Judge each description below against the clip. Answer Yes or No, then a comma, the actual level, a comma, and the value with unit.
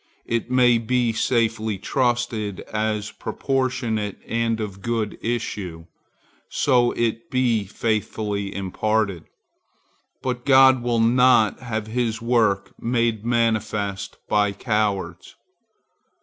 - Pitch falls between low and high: No, low, 115 Hz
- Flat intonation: Yes, narrow, 2.3 semitones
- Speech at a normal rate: No, slow, 100 wpm